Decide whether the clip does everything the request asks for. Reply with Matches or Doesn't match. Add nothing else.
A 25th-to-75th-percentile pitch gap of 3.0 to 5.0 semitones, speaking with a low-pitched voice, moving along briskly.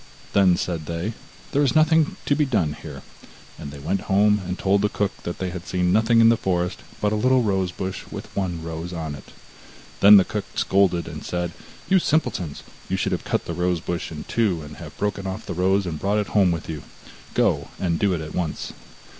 Matches